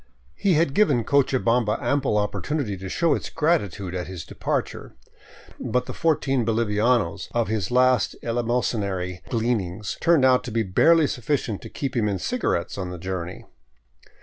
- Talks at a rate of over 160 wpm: No, average, 155 wpm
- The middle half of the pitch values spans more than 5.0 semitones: Yes, wide, 5.6 semitones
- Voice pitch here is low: Yes, low, 115 Hz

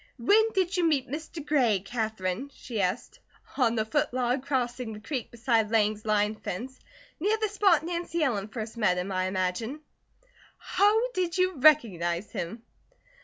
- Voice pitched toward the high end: Yes, high, 240 Hz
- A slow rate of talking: No, average, 160 wpm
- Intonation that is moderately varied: No, wide, 6.6 semitones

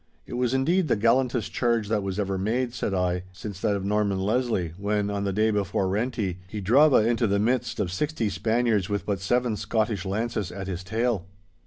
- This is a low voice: Yes, low, 105 Hz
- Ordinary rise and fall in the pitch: Yes, average, 3.5 semitones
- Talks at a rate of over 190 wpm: Yes, average, 200 wpm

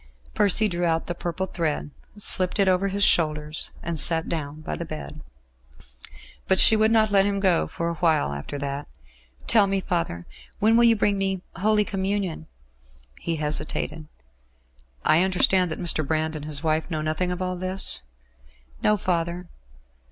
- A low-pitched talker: No, medium, 175 Hz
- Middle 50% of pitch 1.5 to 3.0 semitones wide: No, average, 3.7 semitones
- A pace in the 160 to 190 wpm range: Yes, average, 165 wpm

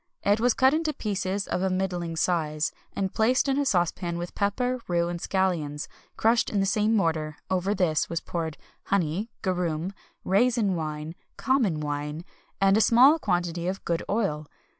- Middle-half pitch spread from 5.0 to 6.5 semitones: No, average, 4.4 semitones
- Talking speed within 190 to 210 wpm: No, average, 165 wpm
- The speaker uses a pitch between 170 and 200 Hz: Yes, medium, 185 Hz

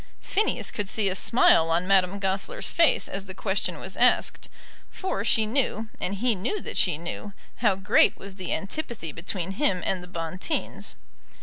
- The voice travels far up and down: No, average, 3.7 semitones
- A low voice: No, high, 195 Hz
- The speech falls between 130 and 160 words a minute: No, average, 175 wpm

